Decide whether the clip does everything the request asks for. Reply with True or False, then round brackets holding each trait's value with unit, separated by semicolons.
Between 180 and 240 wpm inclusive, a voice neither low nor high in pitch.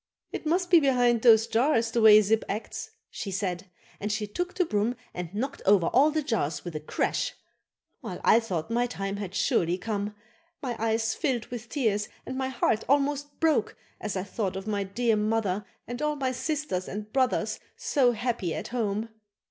False (190 wpm; 225 Hz)